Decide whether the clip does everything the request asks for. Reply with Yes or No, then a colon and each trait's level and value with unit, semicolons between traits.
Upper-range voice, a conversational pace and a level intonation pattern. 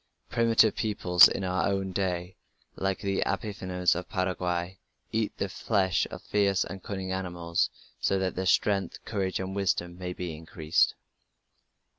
No: very low, 95 Hz; average, 145 wpm; narrow, 1.6 semitones